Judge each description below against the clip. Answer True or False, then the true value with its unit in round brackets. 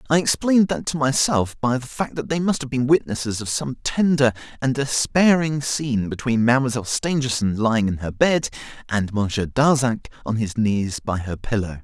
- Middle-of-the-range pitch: False (125 Hz)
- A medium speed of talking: True (180 wpm)